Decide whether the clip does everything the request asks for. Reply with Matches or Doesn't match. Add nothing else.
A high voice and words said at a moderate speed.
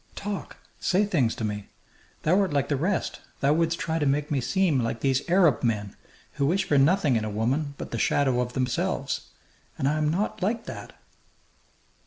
Doesn't match